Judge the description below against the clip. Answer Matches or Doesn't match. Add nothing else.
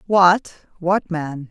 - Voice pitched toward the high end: Doesn't match